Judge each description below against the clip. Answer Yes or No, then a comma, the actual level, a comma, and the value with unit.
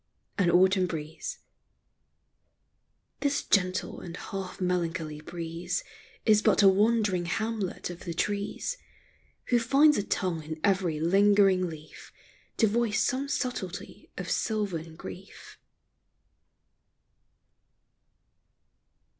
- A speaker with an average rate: No, slow, 100 wpm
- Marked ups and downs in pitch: No, average, 3.8 semitones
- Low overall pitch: No, high, 190 Hz